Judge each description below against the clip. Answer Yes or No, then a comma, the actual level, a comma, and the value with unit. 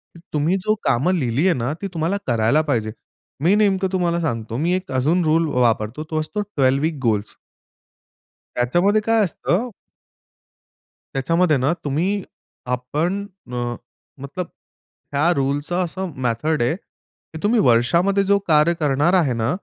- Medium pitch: Yes, medium, 155 Hz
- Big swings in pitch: Yes, wide, 6.1 semitones